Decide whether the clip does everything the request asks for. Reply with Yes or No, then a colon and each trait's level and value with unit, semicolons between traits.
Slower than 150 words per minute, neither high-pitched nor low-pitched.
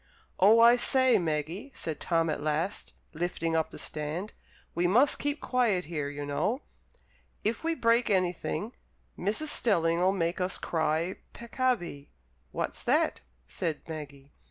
Yes: slow, 135 wpm; medium, 180 Hz